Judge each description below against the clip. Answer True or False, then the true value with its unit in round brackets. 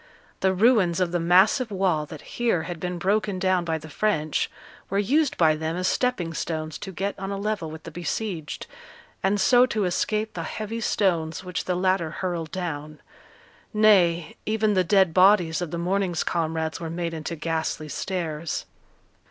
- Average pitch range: True (3.5 semitones)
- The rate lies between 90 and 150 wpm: False (175 wpm)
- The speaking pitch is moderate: True (180 Hz)